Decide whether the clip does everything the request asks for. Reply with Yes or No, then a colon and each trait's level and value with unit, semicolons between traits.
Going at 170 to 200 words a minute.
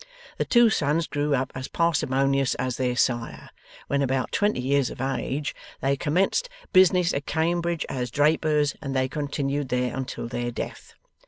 No: average, 160 wpm